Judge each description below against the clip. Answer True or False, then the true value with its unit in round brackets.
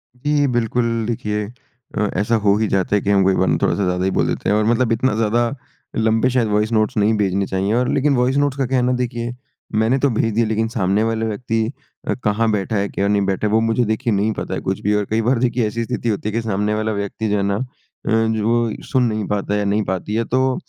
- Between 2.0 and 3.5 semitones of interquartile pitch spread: True (2.4 semitones)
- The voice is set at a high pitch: False (110 Hz)